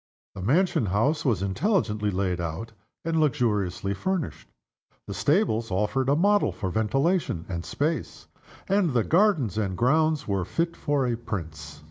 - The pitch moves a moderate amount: No, wide, 8.5 semitones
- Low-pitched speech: Yes, low, 120 Hz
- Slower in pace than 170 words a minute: Yes, average, 145 wpm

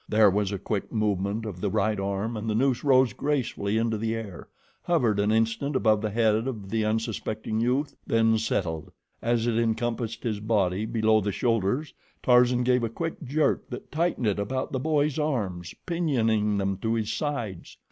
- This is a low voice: Yes, low, 110 Hz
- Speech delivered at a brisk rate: No, average, 180 wpm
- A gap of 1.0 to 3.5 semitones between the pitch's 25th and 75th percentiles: Yes, average, 3.0 semitones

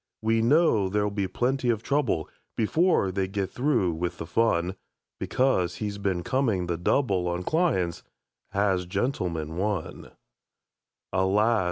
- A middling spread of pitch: Yes, average, 4.7 semitones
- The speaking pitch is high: No, low, 100 Hz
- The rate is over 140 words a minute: No, slow, 135 wpm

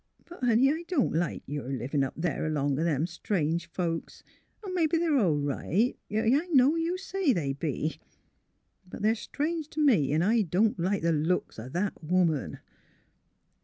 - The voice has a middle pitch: Yes, medium, 180 Hz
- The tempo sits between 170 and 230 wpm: Yes, average, 175 wpm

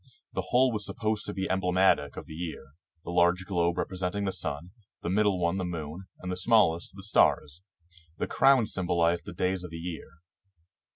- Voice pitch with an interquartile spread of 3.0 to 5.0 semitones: No, narrow, 2.4 semitones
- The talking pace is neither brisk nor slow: Yes, average, 190 wpm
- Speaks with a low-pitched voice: Yes, very low, 90 Hz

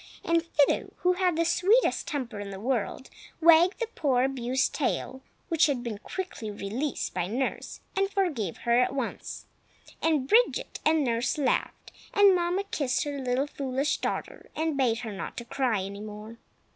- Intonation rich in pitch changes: Yes, wide, 6.0 semitones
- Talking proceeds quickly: No, average, 165 wpm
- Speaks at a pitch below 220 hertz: No, very high, 270 Hz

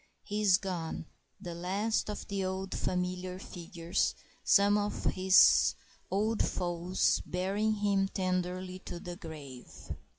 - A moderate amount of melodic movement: No, narrow, 2.0 semitones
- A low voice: No, medium, 185 Hz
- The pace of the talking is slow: Yes, slow, 125 wpm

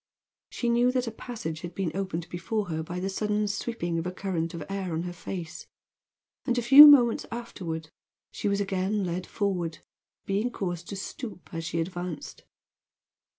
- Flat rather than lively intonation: No, average, 3.9 semitones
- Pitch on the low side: No, high, 190 Hz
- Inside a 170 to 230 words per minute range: Yes, average, 175 wpm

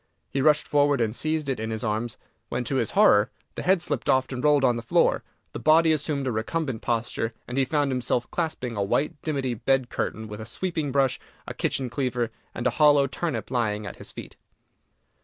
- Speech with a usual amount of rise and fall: Yes, average, 4.1 semitones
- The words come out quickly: Yes, fast, 210 wpm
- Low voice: Yes, low, 130 Hz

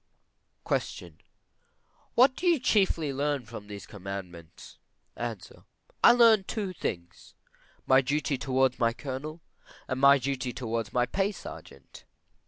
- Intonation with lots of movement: Yes, wide, 6.6 semitones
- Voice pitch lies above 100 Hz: Yes, low, 135 Hz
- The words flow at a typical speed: No, slow, 125 wpm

